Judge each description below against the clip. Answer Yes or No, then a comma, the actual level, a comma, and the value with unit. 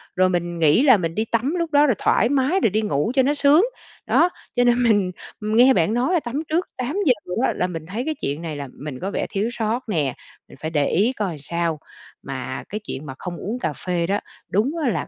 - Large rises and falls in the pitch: Yes, wide, 7.4 semitones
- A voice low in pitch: No, high, 215 Hz